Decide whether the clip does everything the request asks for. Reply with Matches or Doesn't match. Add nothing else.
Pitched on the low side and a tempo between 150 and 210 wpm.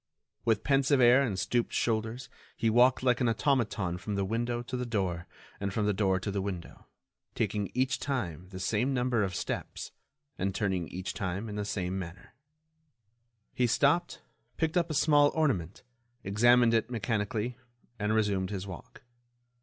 Matches